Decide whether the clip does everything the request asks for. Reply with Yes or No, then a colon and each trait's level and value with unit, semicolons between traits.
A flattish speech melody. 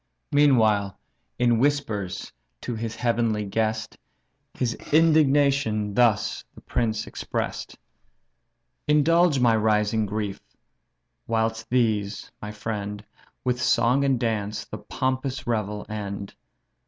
No: average, 3.3 semitones